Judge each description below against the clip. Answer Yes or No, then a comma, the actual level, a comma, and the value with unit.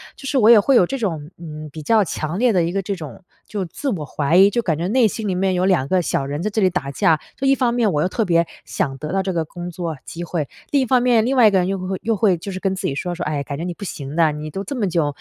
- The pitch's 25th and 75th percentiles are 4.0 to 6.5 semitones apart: Yes, average, 5.0 semitones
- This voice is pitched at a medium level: Yes, medium, 180 Hz